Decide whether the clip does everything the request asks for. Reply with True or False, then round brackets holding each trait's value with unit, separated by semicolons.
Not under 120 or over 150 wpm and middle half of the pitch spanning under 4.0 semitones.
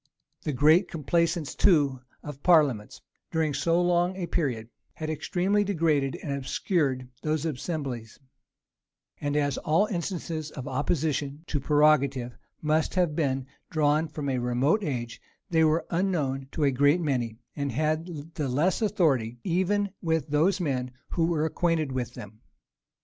True (140 wpm; 3.6 semitones)